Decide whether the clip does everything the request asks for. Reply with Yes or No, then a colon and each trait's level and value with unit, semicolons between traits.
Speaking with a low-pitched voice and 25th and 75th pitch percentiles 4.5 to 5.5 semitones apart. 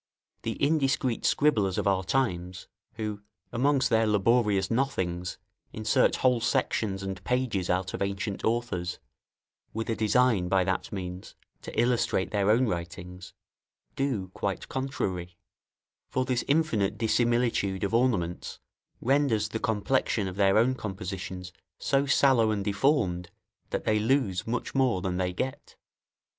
Yes: low, 105 Hz; average, 4.9 semitones